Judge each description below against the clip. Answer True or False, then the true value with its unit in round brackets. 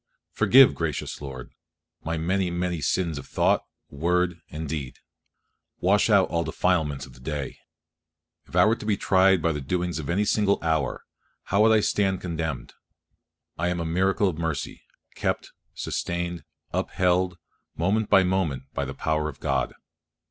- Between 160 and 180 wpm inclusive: True (165 wpm)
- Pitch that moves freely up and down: False (3.2 semitones)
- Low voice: True (85 Hz)